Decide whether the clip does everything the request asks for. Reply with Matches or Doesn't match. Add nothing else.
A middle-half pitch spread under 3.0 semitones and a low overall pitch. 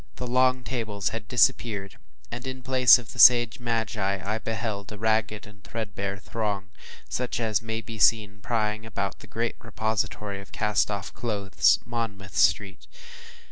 Matches